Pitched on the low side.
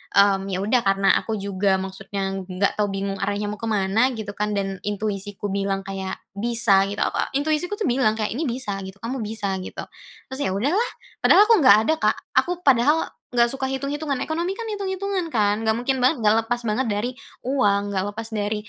No: high, 215 Hz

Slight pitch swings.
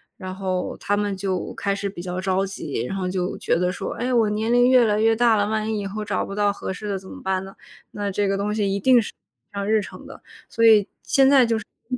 Yes: narrow, 2.2 semitones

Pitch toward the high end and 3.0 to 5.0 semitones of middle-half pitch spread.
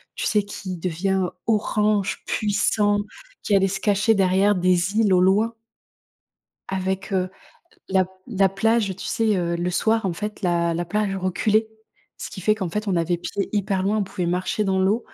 No: high, 195 Hz; narrow, 2.4 semitones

